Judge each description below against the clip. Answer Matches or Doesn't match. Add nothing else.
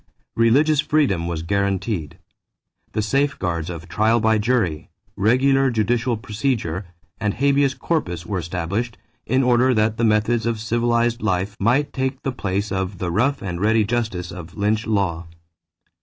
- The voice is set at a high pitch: Doesn't match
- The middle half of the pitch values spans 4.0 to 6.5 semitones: Matches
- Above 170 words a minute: Doesn't match